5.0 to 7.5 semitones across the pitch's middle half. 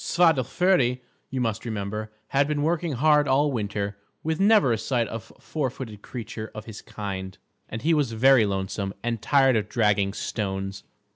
Yes: average, 5.3 semitones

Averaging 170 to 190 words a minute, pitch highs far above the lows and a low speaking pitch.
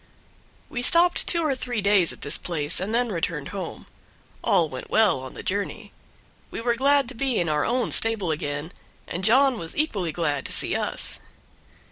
No: average, 185 wpm; wide, 7.1 semitones; high, 205 Hz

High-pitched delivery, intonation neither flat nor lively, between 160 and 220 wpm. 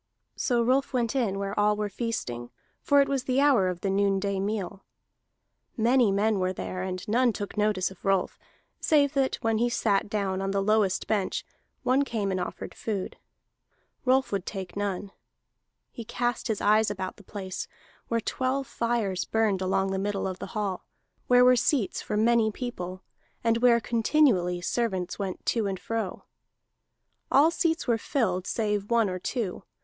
Yes: high, 210 Hz; average, 3.7 semitones; average, 170 wpm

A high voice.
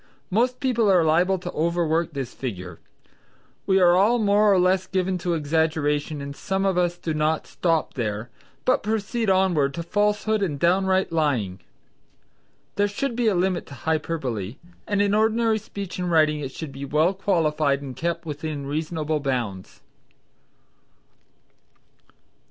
No: medium, 170 Hz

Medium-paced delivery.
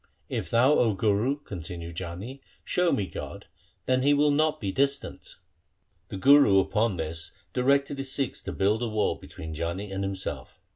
Yes: average, 190 wpm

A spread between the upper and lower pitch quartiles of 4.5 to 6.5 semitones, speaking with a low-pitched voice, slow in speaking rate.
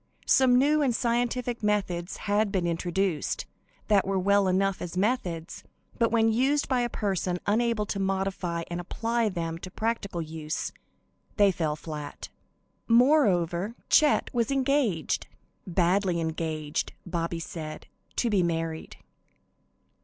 No: wide, 5.4 semitones; high, 195 Hz; slow, 130 wpm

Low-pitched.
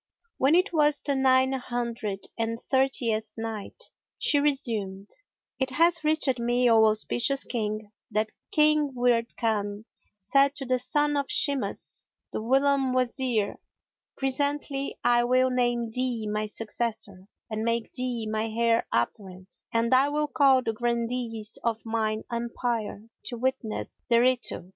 No: high, 240 Hz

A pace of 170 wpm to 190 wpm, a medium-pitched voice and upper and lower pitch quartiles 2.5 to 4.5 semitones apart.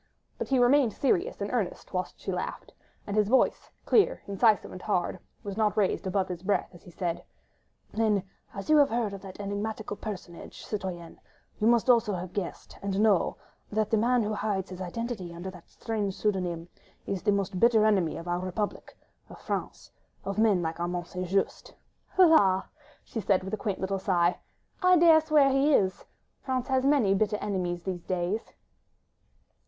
No: average, 180 wpm; high, 200 Hz; average, 3.4 semitones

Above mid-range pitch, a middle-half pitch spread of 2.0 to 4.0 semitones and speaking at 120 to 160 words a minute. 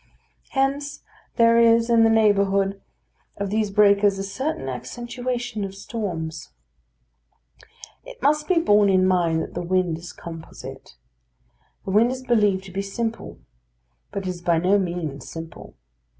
No: high, 200 Hz; average, 4.4 semitones; average, 145 wpm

